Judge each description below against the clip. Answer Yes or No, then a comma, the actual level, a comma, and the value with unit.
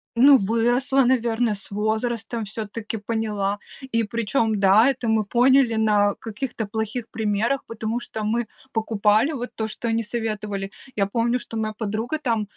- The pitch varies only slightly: Yes, narrow, 2.1 semitones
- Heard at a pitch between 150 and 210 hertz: No, high, 225 Hz